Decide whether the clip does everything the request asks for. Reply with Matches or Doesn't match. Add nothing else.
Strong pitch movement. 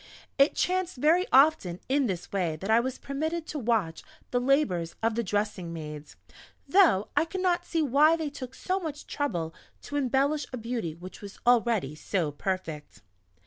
Matches